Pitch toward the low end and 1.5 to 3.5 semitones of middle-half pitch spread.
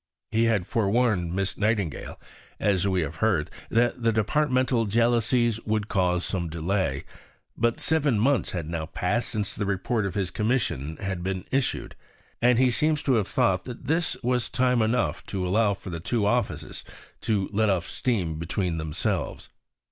No: low, 105 Hz; average, 4.6 semitones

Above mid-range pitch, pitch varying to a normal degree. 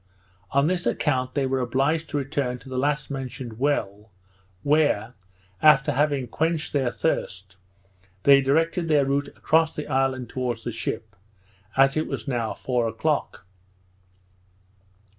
No: low, 135 Hz; average, 3.2 semitones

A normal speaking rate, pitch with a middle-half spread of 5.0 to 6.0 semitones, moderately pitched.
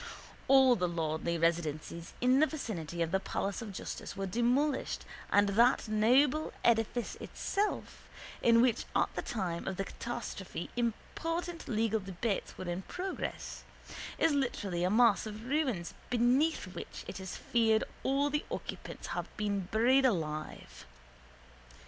No: average, 145 wpm; wide, 5.6 semitones; high, 225 Hz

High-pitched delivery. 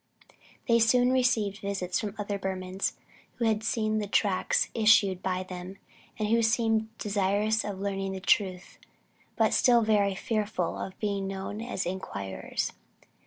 Yes: high, 205 Hz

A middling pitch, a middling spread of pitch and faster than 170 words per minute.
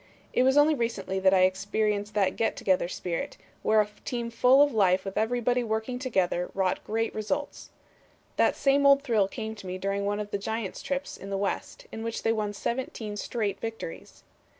No: high, 215 Hz; average, 3.4 semitones; average, 195 wpm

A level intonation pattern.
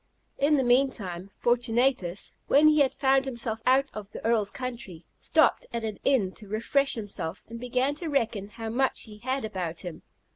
No: average, 4.2 semitones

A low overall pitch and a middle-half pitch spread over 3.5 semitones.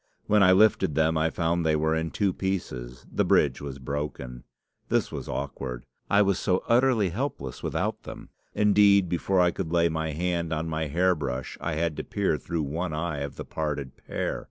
Yes: very low, 80 Hz; average, 3.9 semitones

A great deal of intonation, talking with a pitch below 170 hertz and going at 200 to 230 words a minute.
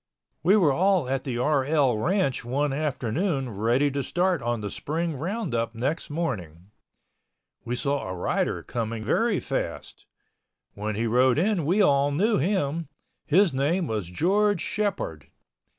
No: wide, 6.7 semitones; medium, 140 Hz; average, 145 wpm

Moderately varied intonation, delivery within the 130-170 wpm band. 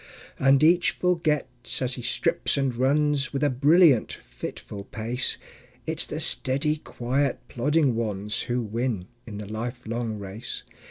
Yes: average, 4.3 semitones; average, 140 wpm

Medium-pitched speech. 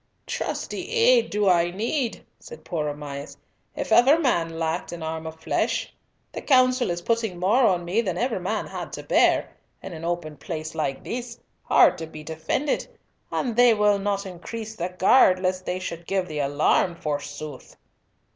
Yes: medium, 180 Hz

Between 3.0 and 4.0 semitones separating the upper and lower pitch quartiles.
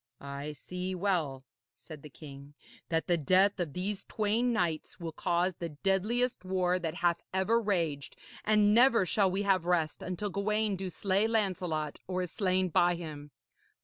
Yes: average, 3.6 semitones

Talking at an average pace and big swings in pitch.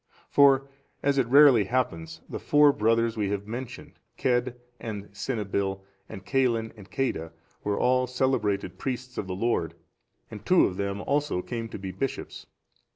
No: average, 155 wpm; average, 4.5 semitones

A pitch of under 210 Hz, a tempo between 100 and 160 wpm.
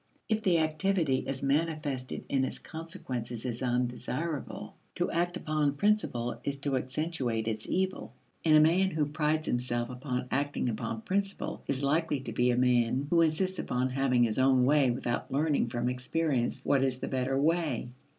No: medium, 140 Hz; average, 170 wpm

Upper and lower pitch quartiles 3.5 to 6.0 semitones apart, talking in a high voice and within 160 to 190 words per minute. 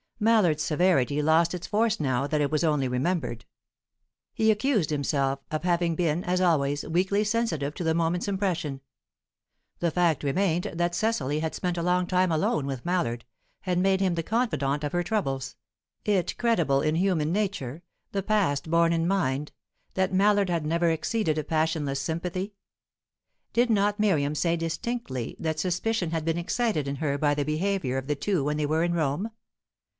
No: average, 4.2 semitones; medium, 170 Hz; average, 175 wpm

